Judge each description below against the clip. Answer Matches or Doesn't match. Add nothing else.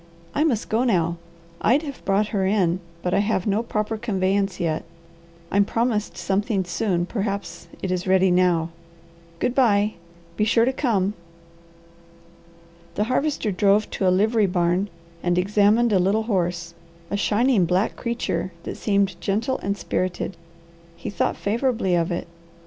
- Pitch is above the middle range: Matches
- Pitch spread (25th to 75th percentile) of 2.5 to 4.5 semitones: Matches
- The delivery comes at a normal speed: Matches